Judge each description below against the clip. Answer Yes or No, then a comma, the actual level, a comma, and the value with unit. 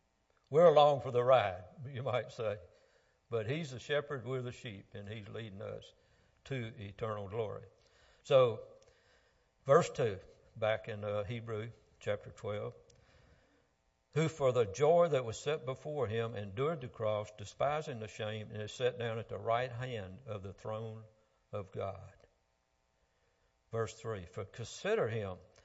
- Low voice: Yes, low, 115 Hz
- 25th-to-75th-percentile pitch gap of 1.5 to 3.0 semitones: No, average, 3.9 semitones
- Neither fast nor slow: Yes, average, 150 wpm